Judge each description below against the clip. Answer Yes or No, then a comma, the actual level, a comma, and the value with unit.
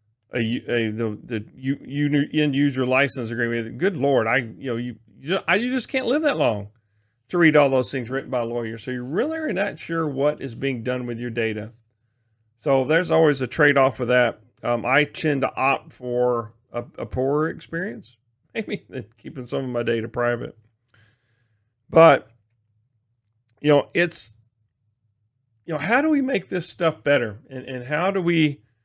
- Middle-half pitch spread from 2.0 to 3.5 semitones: No, average, 4.4 semitones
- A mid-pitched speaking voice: No, low, 125 Hz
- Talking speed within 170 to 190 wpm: Yes, average, 185 wpm